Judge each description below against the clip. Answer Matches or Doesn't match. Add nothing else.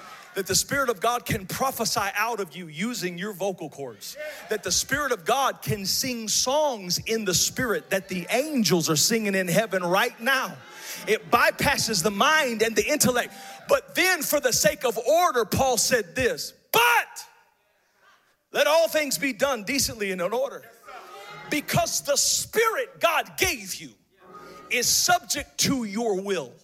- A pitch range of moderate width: Doesn't match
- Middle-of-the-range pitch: Doesn't match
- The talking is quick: Doesn't match